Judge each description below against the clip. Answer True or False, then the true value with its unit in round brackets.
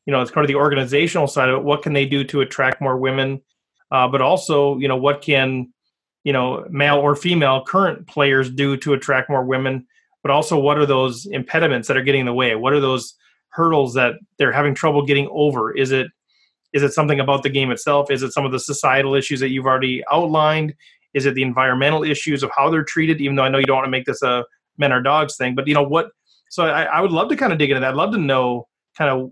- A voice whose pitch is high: False (140 Hz)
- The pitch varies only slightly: True (2.0 semitones)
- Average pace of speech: False (255 wpm)